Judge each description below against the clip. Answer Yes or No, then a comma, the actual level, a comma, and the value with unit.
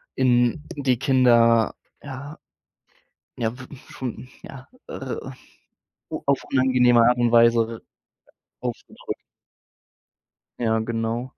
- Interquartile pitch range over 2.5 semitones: No, narrow, 1.9 semitones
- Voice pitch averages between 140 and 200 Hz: No, low, 125 Hz